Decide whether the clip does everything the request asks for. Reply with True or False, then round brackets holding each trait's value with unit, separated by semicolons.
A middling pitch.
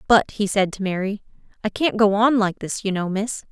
False (205 Hz)